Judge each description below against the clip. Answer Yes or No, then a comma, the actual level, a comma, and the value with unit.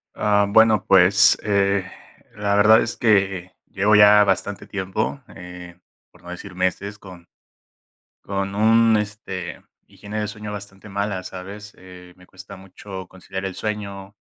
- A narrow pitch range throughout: Yes, narrow, 2.0 semitones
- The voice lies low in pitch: Yes, low, 100 Hz